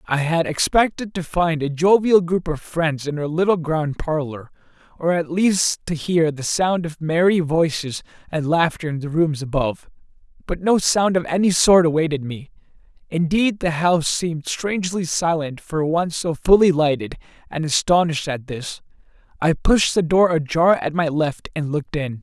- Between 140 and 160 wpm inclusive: No, average, 175 wpm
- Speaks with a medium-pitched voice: Yes, medium, 165 Hz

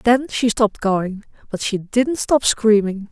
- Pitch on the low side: No, high, 220 Hz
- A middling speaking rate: Yes, average, 175 wpm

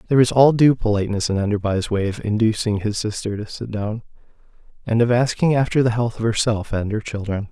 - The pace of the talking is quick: Yes, fast, 210 wpm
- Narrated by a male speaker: Yes, male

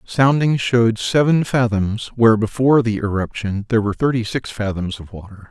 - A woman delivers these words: No, male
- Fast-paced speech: No, average, 165 wpm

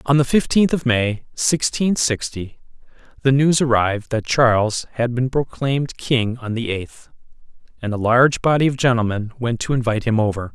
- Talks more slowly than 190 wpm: Yes, average, 170 wpm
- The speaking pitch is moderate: No, low, 125 Hz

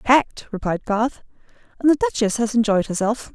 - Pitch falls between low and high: No, high, 230 Hz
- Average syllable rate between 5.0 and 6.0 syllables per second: Yes, 5.3 syllables/s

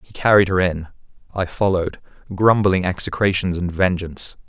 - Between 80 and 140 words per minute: Yes, slow, 135 wpm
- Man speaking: Yes, male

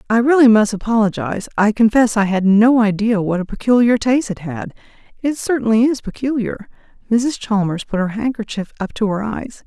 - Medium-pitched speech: No, high, 220 Hz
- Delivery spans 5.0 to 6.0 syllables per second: Yes, 5.4 syllables/s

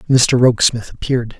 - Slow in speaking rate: Yes, slow, 130 wpm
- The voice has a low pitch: Yes, low, 125 Hz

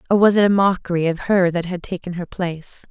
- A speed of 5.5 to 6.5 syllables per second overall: Yes, 6.0 syllables/s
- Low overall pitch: No, medium, 180 Hz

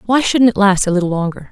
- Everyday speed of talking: No, fast, 280 wpm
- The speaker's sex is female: Yes, female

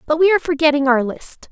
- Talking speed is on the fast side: Yes, fast, 240 wpm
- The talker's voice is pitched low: No, very high, 300 Hz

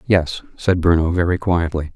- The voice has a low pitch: Yes, very low, 85 Hz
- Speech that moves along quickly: No, average, 155 wpm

